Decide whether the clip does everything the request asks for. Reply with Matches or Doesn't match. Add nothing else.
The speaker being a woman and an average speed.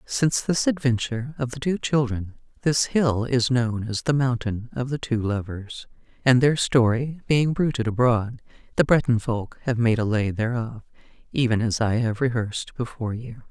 Matches